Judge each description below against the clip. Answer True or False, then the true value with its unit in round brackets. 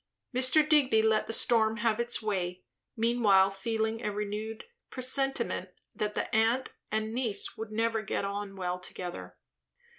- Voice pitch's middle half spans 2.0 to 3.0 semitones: True (2.7 semitones)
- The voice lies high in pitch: True (220 Hz)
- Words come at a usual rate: True (145 wpm)